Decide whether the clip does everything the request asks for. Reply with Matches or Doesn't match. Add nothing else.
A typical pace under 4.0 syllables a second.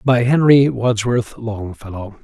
Matches